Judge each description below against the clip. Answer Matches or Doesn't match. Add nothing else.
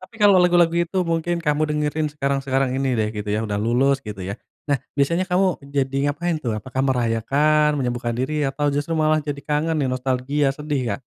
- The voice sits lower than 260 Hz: Matches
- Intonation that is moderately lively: Matches